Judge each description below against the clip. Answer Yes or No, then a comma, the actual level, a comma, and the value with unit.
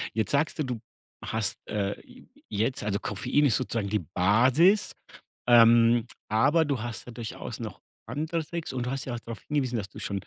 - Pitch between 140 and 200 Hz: No, low, 120 Hz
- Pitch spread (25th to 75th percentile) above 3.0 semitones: Yes, average, 4.6 semitones